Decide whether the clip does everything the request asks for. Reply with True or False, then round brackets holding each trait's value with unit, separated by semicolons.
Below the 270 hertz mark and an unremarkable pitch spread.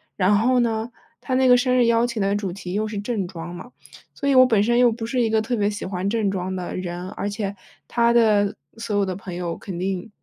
True (210 Hz; 3.7 semitones)